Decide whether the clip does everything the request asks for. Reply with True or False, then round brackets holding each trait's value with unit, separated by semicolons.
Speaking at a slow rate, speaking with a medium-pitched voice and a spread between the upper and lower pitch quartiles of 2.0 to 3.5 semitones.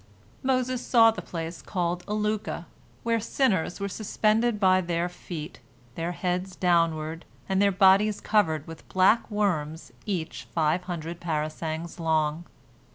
False (130 wpm; 180 Hz; 4.3 semitones)